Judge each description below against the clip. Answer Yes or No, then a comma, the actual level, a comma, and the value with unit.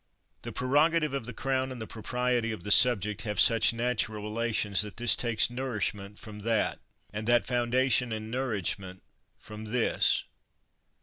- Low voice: Yes, low, 115 Hz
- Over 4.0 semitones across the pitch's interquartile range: No, average, 2.8 semitones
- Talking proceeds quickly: No, average, 160 wpm